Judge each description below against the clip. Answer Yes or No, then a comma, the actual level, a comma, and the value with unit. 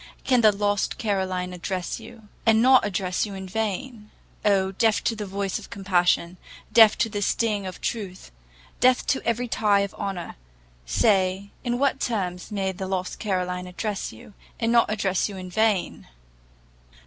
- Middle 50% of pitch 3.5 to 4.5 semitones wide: No, average, 3.0 semitones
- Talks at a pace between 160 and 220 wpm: Yes, average, 165 wpm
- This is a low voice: No, high, 200 Hz